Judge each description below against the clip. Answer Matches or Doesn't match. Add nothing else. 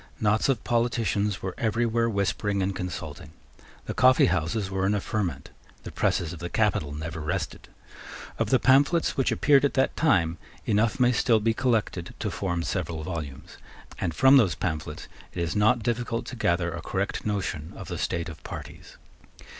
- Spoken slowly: Doesn't match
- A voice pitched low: Matches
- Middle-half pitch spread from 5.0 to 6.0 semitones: Matches